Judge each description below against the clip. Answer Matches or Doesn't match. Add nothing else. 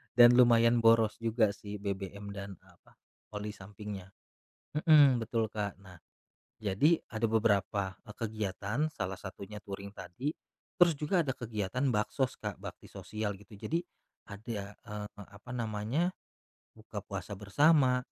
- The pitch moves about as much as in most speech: Matches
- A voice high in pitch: Doesn't match